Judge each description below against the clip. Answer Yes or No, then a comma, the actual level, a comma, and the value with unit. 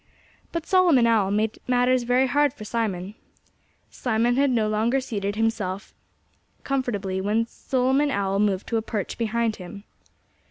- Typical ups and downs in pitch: Yes, average, 3.7 semitones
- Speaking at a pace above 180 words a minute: No, average, 145 wpm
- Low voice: No, high, 225 Hz